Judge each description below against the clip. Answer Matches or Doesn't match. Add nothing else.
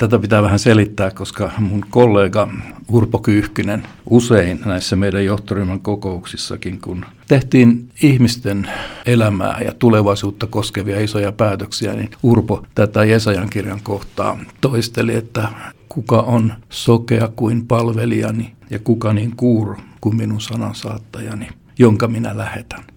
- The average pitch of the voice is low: Matches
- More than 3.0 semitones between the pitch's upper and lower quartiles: Doesn't match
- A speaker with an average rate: Matches